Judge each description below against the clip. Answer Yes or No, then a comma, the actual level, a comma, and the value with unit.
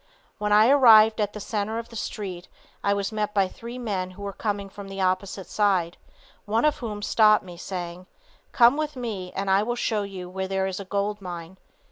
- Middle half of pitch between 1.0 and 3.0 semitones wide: Yes, narrow, 2.4 semitones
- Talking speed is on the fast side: Yes, fast, 210 wpm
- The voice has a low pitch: No, high, 200 Hz